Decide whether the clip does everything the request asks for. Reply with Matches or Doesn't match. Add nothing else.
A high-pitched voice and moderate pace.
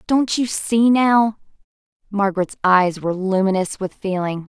Doesn't match